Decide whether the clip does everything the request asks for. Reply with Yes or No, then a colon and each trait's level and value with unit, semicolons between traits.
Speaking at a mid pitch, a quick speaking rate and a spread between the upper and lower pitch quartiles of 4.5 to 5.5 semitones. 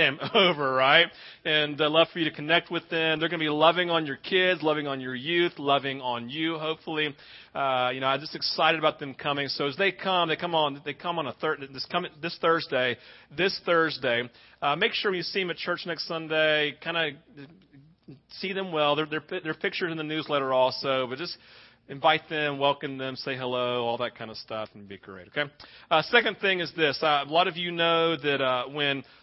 No: medium, 155 Hz; fast, 220 wpm; average, 3.4 semitones